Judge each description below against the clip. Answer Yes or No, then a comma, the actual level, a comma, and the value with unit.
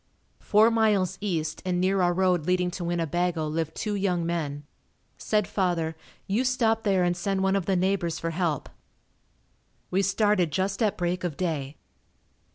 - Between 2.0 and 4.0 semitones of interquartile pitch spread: Yes, average, 2.7 semitones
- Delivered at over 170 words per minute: No, average, 165 wpm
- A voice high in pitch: No, medium, 180 Hz